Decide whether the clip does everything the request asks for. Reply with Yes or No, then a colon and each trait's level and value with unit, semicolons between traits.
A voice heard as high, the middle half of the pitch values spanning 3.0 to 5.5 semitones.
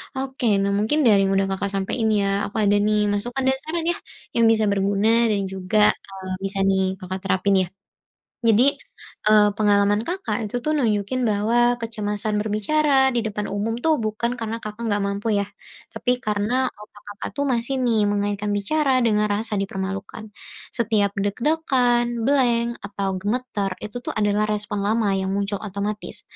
No: high, 210 Hz; narrow, 2.6 semitones